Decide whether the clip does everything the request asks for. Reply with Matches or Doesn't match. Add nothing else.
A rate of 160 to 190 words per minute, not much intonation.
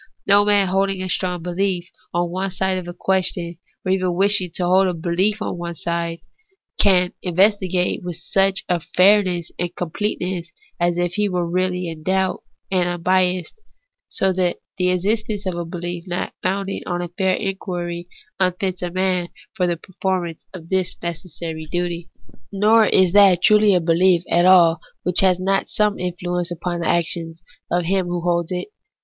Matches